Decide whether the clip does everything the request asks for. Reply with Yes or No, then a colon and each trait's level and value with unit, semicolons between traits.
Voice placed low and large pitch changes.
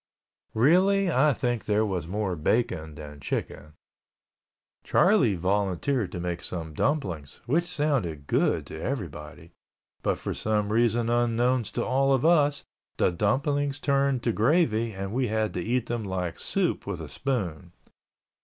Yes: low, 110 Hz; wide, 7.3 semitones